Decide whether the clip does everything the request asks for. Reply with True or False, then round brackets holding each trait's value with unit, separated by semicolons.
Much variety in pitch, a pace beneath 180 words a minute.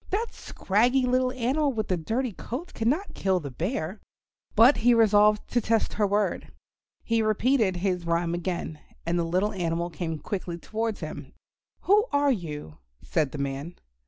True (6.0 semitones; 160 wpm)